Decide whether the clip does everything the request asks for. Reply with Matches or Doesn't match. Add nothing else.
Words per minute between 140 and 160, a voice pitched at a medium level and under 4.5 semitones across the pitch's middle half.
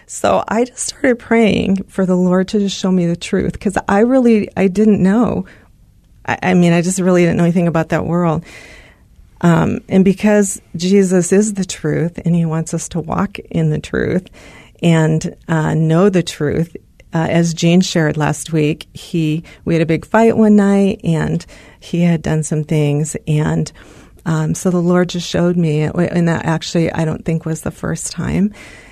Doesn't match